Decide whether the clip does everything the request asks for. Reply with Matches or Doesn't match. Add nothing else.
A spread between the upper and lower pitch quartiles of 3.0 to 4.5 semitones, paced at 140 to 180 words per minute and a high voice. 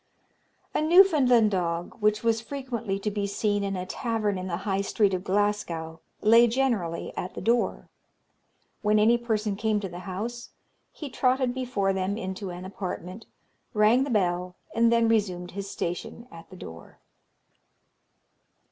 Matches